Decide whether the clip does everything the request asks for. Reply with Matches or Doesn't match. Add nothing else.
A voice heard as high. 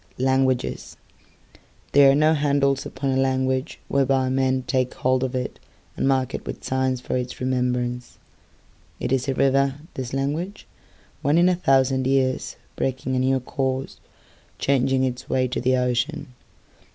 Doesn't match